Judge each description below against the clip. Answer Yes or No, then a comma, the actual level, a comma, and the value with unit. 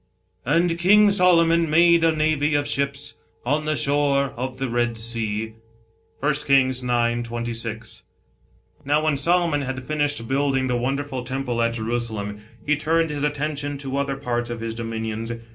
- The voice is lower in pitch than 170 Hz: Yes, medium, 140 Hz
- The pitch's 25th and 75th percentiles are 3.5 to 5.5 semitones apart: Yes, average, 4.1 semitones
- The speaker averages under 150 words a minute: No, average, 160 wpm